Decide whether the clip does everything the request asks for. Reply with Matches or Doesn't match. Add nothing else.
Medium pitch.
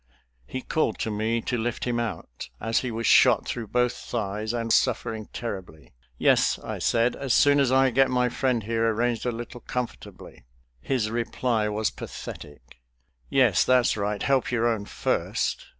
Doesn't match